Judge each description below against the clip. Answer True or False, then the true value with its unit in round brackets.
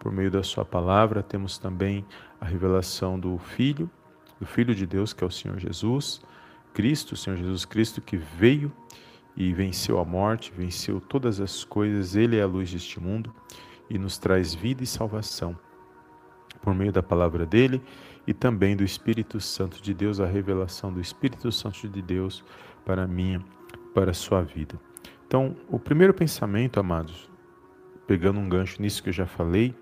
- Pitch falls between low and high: False (95 Hz)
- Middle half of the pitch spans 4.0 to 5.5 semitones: False (3.5 semitones)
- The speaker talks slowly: False (170 wpm)